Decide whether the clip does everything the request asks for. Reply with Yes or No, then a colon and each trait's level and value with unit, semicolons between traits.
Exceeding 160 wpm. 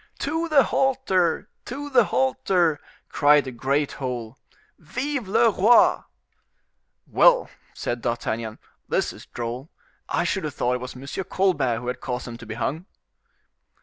No: average, 150 wpm